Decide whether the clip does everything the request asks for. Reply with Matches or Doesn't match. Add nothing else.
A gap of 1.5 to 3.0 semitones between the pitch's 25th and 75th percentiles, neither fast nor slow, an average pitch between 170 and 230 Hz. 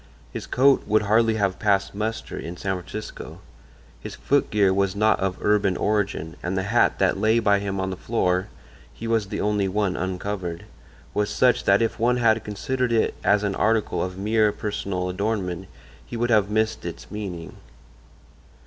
Doesn't match